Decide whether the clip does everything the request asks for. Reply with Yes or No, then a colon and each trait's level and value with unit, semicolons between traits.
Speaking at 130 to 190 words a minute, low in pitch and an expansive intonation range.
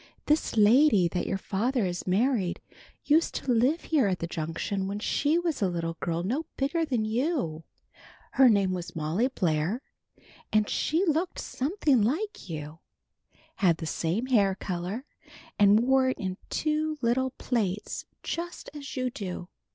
No: average, 155 wpm; high, 220 Hz; wide, 7.4 semitones